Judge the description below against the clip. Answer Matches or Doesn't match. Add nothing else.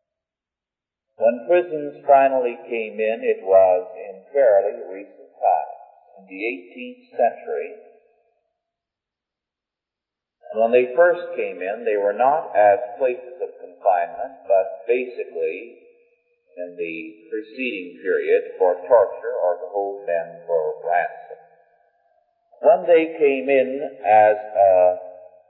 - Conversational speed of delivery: Doesn't match